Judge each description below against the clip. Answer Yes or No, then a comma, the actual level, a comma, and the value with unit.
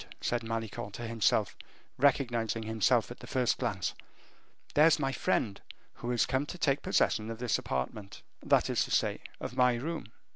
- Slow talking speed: No, average, 170 wpm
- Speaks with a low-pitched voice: Yes, low, 120 Hz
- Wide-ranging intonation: No, average, 3.3 semitones